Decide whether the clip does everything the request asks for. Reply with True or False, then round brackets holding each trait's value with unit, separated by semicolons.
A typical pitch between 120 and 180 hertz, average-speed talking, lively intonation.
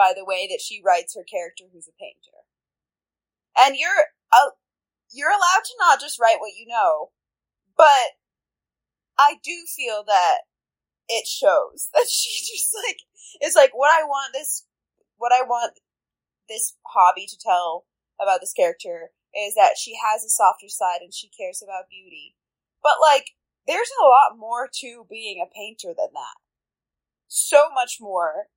False (265 Hz; 160 wpm; 7.7 semitones)